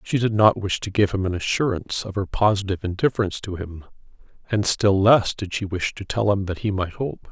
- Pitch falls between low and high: No, low, 100 Hz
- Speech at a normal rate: No, fast, 220 wpm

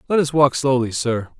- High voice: No, low, 135 Hz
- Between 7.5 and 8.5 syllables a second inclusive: No, 5.2 syllables/s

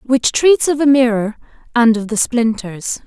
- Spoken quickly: No, average, 175 wpm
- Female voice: Yes, female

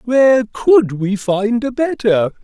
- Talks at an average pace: Yes, average, 150 wpm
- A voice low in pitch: No, high, 230 Hz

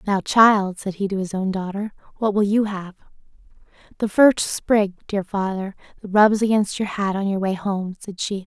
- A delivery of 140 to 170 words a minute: No, average, 195 wpm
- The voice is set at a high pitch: Yes, high, 200 Hz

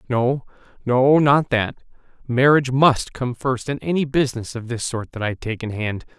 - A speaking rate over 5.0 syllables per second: No, 4.8 syllables/s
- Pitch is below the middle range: Yes, low, 125 Hz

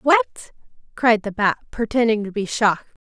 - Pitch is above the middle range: Yes, high, 220 Hz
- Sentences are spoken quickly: No, average, 155 wpm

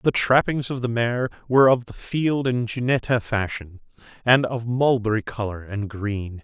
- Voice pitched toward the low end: Yes, low, 115 Hz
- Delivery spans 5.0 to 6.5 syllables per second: No, 4.6 syllables/s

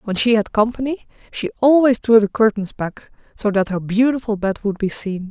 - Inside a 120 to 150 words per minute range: No, fast, 205 wpm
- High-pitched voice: Yes, high, 220 Hz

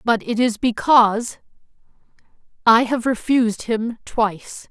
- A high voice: Yes, high, 230 Hz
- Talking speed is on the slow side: Yes, slow, 100 wpm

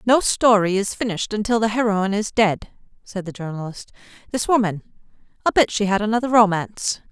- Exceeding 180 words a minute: No, average, 160 wpm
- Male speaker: No, female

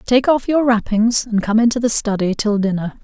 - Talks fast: Yes, fast, 220 wpm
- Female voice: Yes, female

